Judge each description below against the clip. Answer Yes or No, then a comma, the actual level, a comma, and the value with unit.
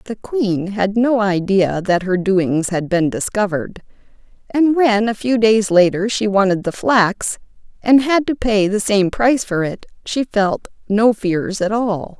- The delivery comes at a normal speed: Yes, average, 175 wpm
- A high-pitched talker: Yes, high, 205 Hz